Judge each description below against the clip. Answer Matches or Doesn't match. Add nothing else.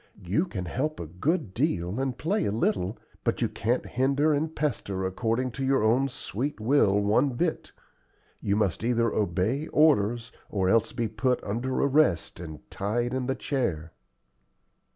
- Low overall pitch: Matches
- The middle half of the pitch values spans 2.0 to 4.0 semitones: Doesn't match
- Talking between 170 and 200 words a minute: Doesn't match